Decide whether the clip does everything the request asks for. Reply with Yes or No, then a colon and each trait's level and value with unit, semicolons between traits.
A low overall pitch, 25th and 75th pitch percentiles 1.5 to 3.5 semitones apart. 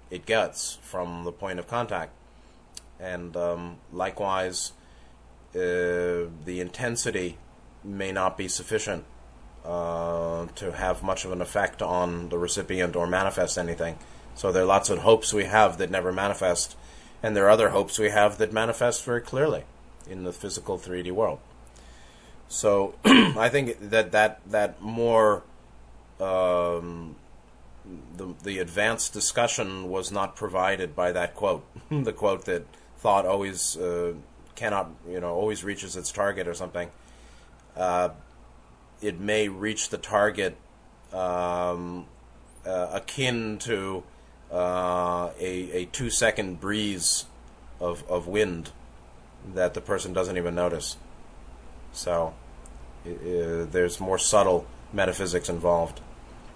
Yes: very low, 90 Hz; average, 2.9 semitones